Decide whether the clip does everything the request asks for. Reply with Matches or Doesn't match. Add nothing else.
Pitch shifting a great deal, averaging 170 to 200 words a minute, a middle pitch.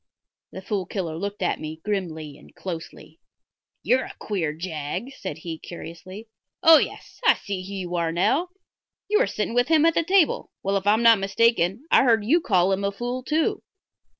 Doesn't match